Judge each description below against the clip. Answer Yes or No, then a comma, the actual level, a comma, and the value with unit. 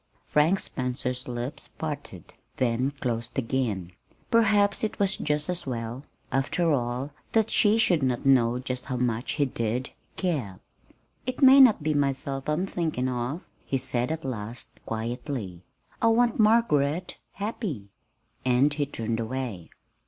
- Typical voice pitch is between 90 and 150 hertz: Yes, low, 135 Hz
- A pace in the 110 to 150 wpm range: Yes, average, 140 wpm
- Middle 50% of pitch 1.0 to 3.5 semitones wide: No, wide, 5.4 semitones